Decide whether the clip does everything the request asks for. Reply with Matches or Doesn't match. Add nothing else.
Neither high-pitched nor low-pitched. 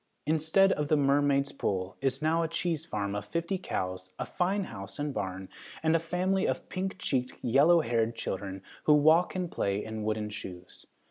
Matches